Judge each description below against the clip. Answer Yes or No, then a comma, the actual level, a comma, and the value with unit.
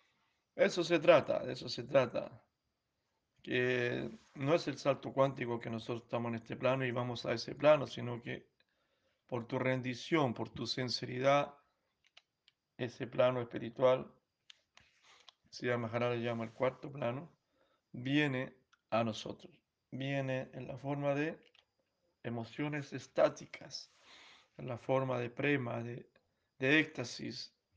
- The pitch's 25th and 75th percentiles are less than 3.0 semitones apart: Yes, narrow, 2.5 semitones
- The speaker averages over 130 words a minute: No, slow, 125 wpm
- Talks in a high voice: No, low, 130 Hz